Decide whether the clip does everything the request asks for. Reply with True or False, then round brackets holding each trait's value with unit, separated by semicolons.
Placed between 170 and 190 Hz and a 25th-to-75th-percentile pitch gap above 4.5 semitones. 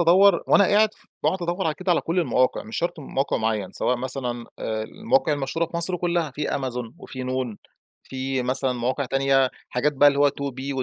False (135 Hz; 5.0 semitones)